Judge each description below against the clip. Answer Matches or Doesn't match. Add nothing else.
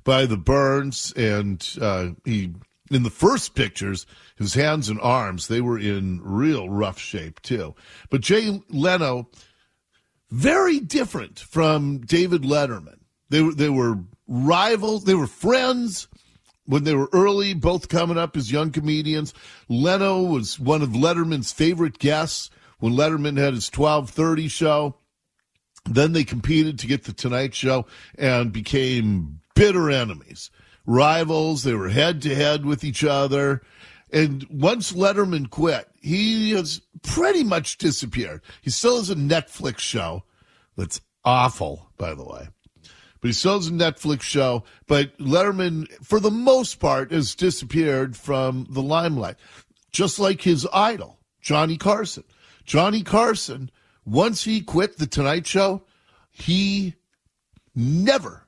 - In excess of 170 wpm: Doesn't match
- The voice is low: Doesn't match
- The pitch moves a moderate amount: Doesn't match